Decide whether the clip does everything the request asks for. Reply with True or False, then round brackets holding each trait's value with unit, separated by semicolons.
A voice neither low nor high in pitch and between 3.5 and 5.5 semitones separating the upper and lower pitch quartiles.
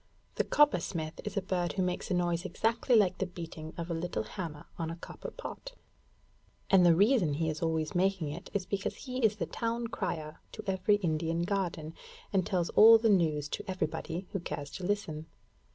True (180 Hz; 3.8 semitones)